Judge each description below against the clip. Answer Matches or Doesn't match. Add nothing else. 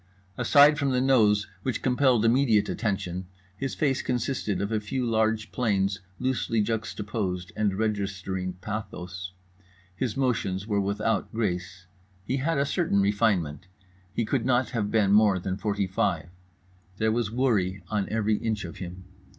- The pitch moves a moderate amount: Matches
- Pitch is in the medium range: Doesn't match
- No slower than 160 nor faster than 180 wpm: Doesn't match